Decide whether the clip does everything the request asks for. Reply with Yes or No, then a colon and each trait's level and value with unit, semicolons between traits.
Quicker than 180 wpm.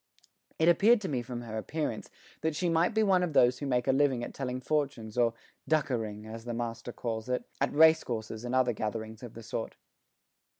Yes: fast, 205 wpm